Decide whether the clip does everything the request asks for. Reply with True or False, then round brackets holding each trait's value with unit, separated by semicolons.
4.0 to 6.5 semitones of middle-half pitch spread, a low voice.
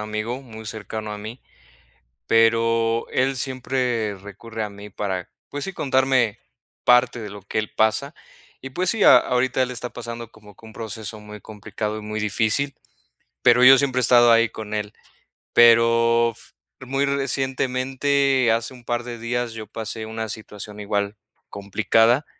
False (2.9 semitones; 115 Hz)